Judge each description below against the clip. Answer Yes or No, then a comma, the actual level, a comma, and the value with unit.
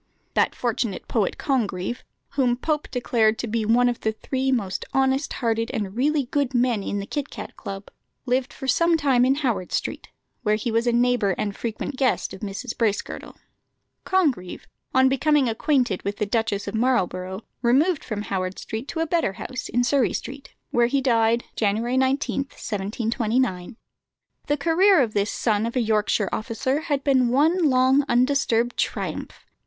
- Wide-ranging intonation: No, average, 3.7 semitones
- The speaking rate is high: No, average, 170 wpm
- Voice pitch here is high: Yes, high, 245 Hz